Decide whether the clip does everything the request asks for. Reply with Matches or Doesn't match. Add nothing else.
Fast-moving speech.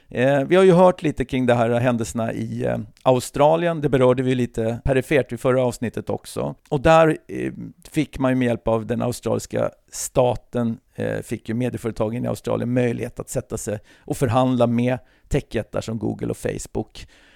Doesn't match